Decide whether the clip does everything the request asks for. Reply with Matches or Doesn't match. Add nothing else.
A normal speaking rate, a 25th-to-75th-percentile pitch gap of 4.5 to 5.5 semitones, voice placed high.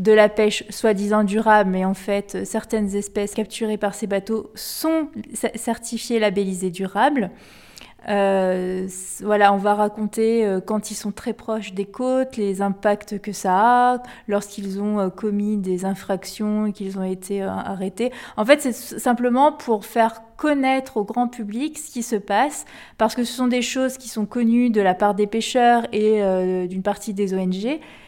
Doesn't match